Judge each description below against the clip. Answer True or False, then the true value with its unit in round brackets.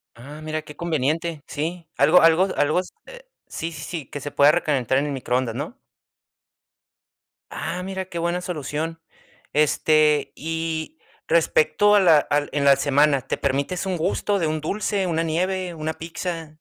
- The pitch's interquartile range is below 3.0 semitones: False (3.4 semitones)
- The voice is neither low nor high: True (160 Hz)